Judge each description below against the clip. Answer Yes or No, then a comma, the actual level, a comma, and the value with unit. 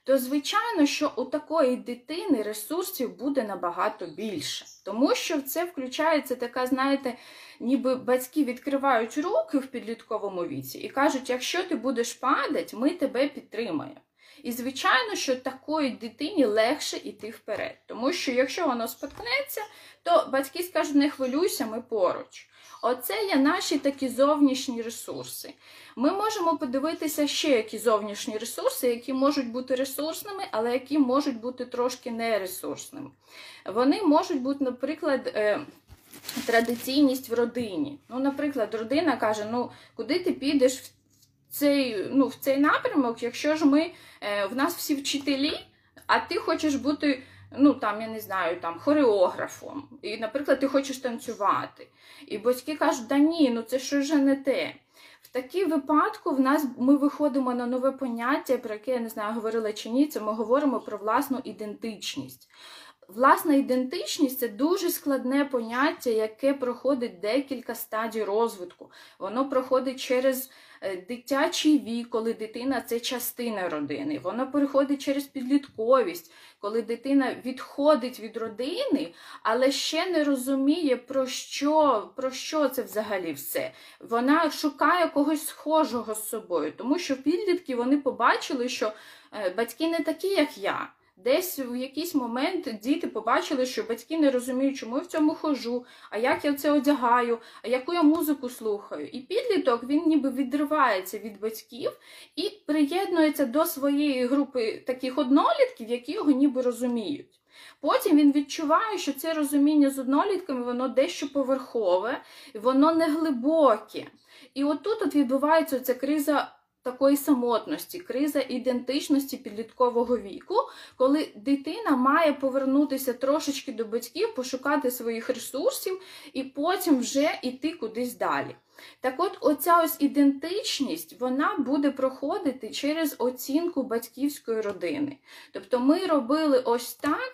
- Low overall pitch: No, very high, 275 Hz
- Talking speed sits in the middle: Yes, average, 135 wpm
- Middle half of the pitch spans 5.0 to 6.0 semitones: No, average, 3.8 semitones